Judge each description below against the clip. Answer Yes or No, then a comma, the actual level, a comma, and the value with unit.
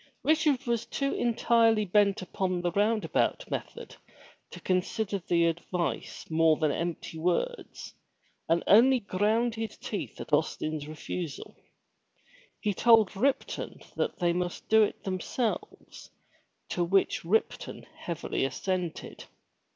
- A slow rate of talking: Yes, slow, 120 wpm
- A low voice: No, high, 195 Hz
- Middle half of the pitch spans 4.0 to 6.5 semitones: Yes, average, 4.7 semitones